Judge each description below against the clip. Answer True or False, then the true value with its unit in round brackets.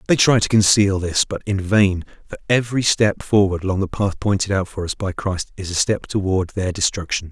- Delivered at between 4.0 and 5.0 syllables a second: False (5.3 syllables/s)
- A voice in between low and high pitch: False (100 Hz)